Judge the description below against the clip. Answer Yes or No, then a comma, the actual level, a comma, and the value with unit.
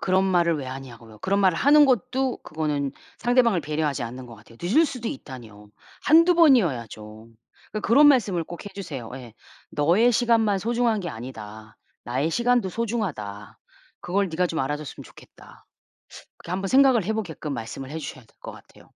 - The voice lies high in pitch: No, medium, 175 Hz